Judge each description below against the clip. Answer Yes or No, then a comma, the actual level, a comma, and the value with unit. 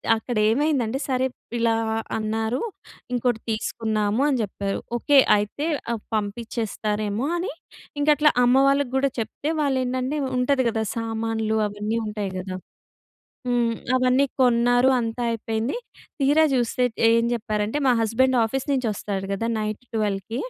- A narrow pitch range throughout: No, average, 3.2 semitones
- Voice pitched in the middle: No, high, 230 Hz